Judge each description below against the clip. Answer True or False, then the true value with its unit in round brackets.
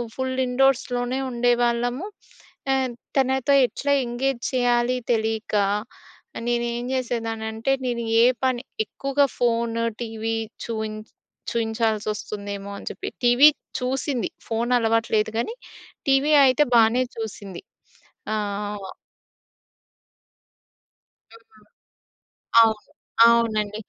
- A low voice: False (240 Hz)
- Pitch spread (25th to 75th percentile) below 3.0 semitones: True (2.5 semitones)